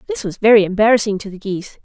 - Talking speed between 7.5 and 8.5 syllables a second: Yes, 7.8 syllables/s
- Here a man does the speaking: No, female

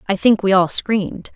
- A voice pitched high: Yes, high, 195 Hz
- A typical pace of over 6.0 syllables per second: No, 5.1 syllables/s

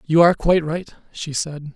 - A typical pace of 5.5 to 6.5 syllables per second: Yes, 5.9 syllables/s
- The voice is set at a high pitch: No, medium, 160 Hz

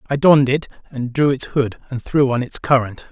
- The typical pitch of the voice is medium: No, low, 130 Hz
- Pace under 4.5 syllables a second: No, 5.4 syllables/s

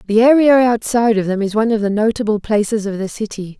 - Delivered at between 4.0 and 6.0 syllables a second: No, 6.5 syllables/s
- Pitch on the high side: Yes, high, 215 Hz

